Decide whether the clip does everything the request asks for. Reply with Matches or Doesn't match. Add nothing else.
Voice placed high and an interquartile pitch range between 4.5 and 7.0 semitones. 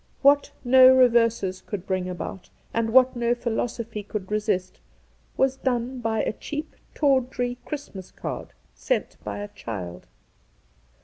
Doesn't match